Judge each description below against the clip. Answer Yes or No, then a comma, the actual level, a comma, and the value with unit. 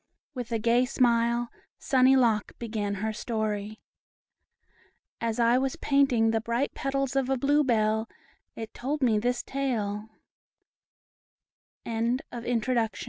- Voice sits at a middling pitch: No, high, 235 Hz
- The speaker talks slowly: No, average, 150 wpm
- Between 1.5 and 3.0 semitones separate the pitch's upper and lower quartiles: Yes, average, 2.7 semitones